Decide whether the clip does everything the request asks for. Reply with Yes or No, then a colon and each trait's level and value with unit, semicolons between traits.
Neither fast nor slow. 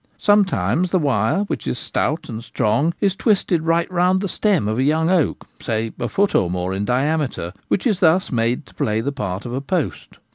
No: fast, 210 wpm